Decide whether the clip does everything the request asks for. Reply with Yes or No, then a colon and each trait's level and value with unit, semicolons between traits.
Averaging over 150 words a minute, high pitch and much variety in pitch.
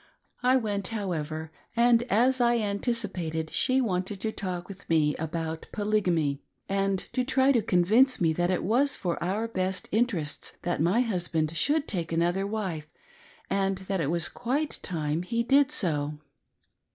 Yes: average, 160 wpm; high, 195 Hz; wide, 5.7 semitones